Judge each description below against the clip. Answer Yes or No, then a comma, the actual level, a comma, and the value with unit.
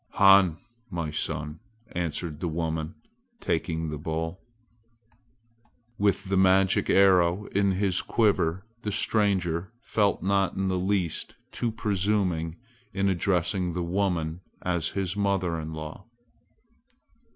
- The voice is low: Yes, very low, 90 Hz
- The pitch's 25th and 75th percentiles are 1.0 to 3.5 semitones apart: Yes, average, 3.1 semitones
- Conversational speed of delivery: No, slow, 120 wpm